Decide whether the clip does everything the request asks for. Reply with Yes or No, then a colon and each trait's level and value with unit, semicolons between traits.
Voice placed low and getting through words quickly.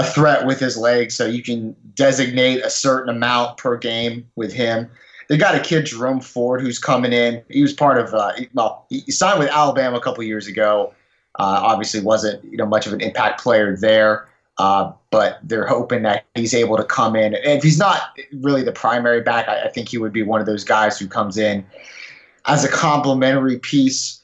Yes: low, 120 Hz; fast, 215 wpm